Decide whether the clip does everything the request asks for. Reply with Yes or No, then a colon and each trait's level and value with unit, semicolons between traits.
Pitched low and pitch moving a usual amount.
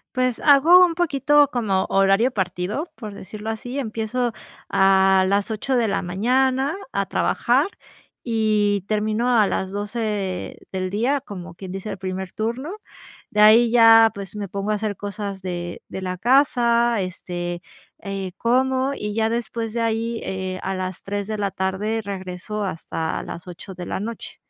No: high, 210 Hz; average, 3.7 semitones